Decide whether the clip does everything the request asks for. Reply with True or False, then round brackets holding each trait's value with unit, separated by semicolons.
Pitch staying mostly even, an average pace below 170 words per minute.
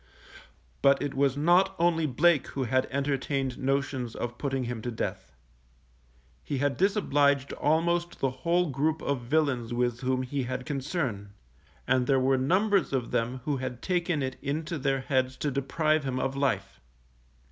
False (3.0 semitones; 160 wpm)